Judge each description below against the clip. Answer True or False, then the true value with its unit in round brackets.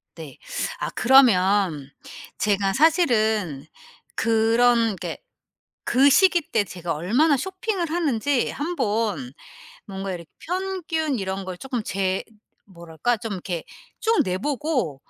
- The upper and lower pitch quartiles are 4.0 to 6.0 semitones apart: False (7.6 semitones)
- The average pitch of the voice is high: True (225 Hz)